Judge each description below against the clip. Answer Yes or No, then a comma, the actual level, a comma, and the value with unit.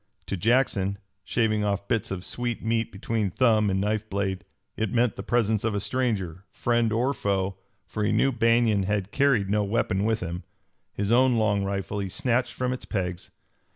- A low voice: Yes, low, 105 Hz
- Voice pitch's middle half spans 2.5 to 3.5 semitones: Yes, average, 3.1 semitones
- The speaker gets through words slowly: No, average, 185 wpm